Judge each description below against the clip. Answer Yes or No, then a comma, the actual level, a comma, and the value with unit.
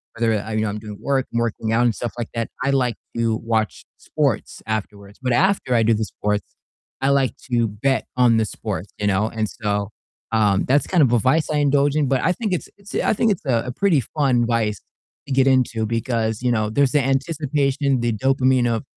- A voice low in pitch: Yes, low, 120 Hz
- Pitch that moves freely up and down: No, average, 3.8 semitones